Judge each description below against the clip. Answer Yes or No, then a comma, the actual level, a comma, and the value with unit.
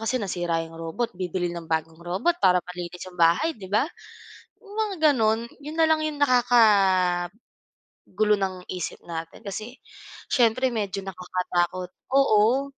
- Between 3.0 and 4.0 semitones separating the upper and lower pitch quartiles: No, wide, 5.5 semitones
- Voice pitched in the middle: No, high, 195 Hz